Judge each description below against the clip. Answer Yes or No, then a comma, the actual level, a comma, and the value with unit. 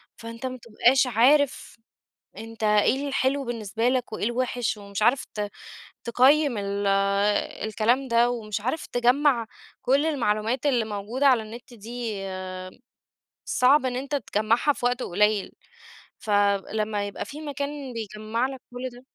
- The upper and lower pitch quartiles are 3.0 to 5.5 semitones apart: Yes, average, 3.4 semitones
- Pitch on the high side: Yes, high, 240 Hz